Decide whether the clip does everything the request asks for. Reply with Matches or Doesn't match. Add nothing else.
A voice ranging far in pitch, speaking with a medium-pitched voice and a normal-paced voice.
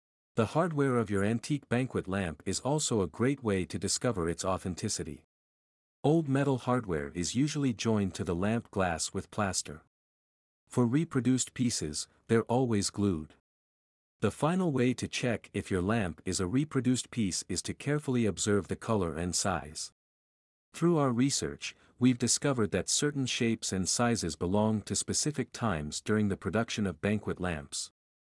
Doesn't match